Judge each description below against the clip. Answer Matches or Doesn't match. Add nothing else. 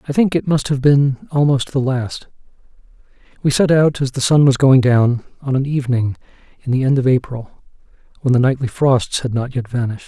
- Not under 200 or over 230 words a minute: Matches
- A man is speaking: Matches